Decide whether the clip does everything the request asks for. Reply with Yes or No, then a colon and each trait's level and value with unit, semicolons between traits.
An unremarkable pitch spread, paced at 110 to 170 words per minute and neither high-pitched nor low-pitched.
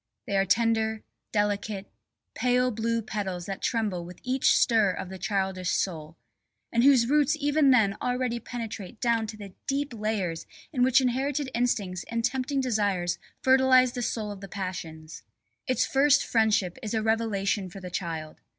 No: average, 4.5 semitones; average, 160 wpm; high, 220 Hz